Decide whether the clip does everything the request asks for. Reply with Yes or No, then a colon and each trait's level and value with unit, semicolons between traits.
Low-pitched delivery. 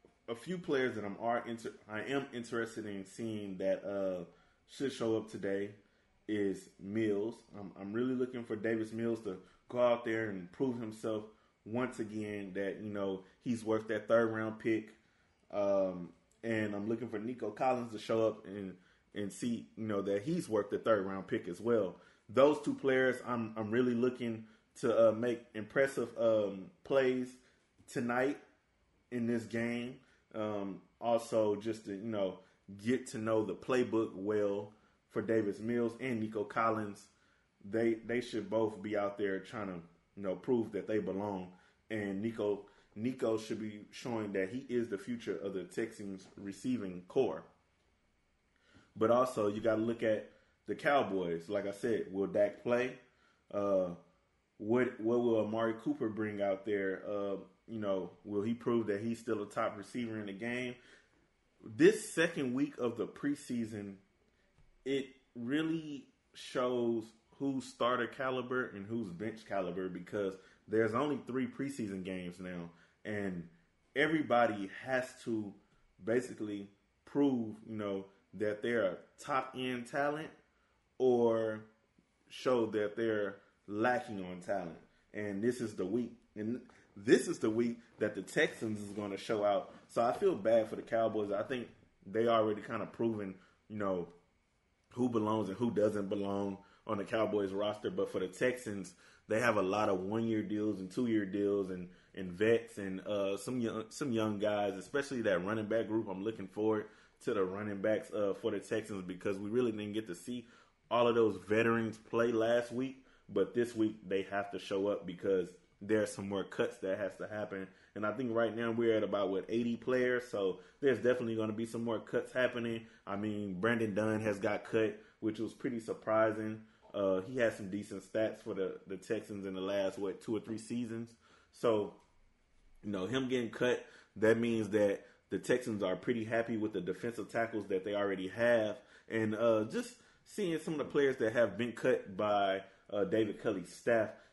Yes: low, 110 Hz